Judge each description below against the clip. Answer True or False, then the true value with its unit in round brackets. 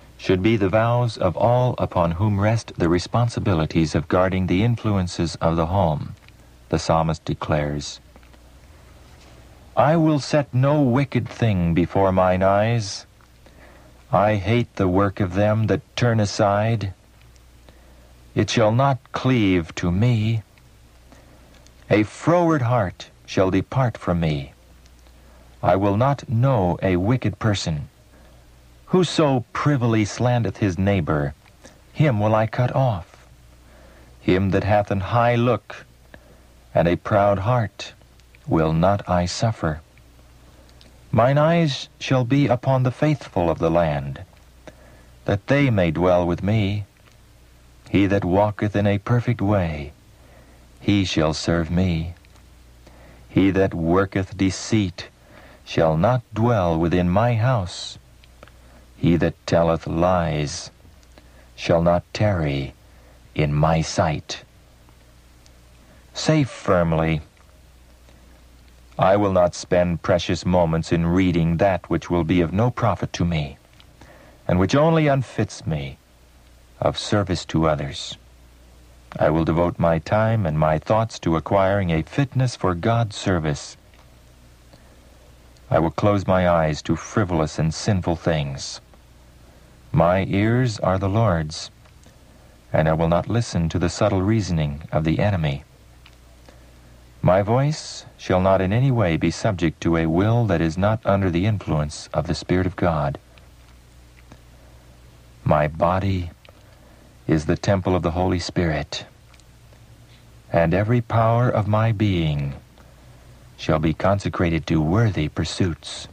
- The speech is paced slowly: True (125 wpm)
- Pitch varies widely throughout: True (9.0 semitones)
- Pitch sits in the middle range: False (85 Hz)